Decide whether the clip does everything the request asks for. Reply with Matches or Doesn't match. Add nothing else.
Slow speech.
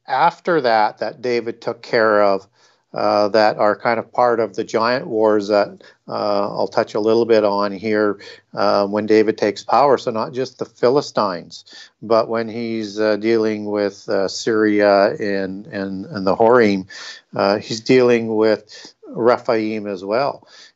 Doesn't match